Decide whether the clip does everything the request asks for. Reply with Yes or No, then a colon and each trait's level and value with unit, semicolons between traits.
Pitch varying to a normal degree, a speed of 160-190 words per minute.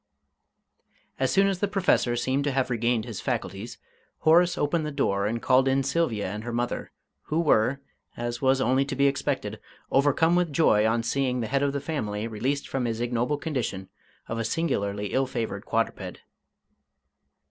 Yes: average, 3.8 semitones; average, 175 wpm